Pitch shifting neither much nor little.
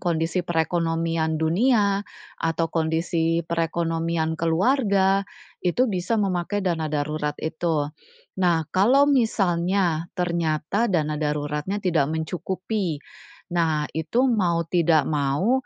Yes: average, 3.1 semitones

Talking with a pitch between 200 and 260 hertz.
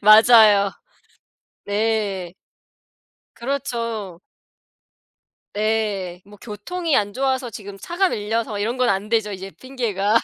Yes: high, 215 Hz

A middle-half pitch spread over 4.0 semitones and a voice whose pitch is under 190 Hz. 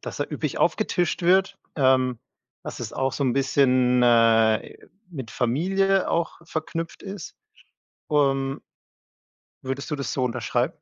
Yes: average, 4.8 semitones; low, 135 Hz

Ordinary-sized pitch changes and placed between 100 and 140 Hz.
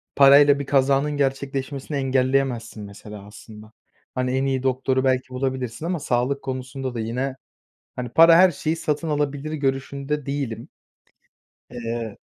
No: narrow, 1.9 semitones; low, 135 Hz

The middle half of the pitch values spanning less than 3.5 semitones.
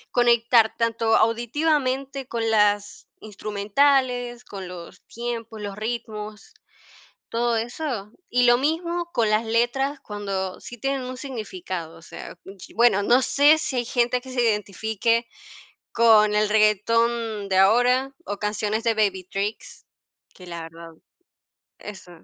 Yes: average, 3.0 semitones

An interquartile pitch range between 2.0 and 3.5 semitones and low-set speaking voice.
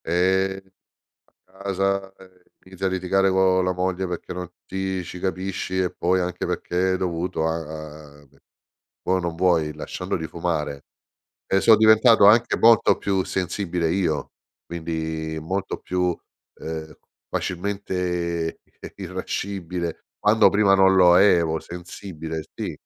Yes: narrow, 2.5 semitones; very low, 90 Hz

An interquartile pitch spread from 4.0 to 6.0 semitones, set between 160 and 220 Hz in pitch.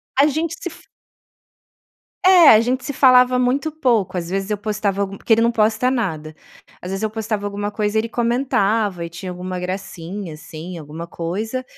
Yes: average, 5.2 semitones; high, 210 Hz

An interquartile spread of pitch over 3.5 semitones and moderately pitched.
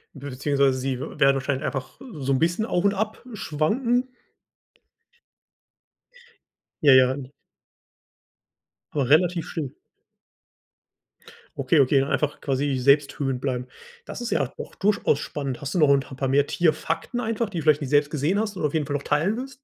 Yes: average, 4.4 semitones; medium, 145 Hz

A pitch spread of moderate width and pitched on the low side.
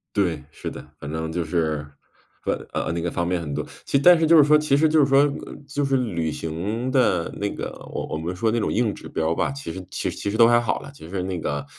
No: wide, 8.9 semitones; low, 100 Hz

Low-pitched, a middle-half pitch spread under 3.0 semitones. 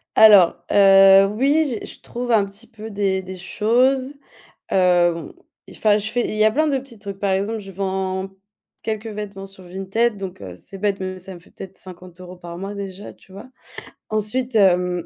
No: high, 195 Hz; narrow, 2.5 semitones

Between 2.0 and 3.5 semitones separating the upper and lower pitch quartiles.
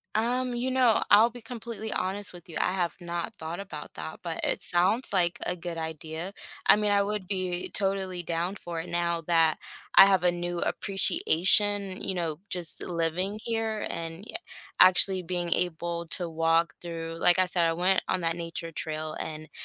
Yes: average, 3.0 semitones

